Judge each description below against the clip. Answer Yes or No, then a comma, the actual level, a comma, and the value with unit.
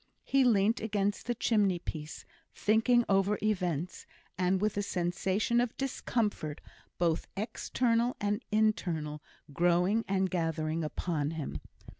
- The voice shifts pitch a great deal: No, average, 4.2 semitones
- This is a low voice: No, high, 195 Hz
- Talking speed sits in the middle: No, slow, 120 wpm